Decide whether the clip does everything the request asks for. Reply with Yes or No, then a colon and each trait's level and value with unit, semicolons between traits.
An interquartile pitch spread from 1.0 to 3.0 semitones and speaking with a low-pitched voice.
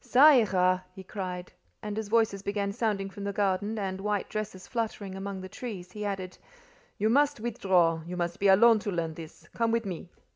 No: average, 2.7 semitones; high, 200 Hz